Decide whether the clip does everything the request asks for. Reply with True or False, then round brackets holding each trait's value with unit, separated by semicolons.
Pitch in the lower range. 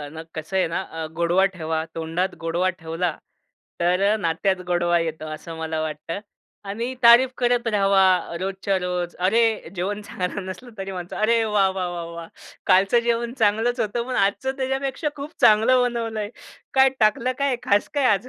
False (195 Hz)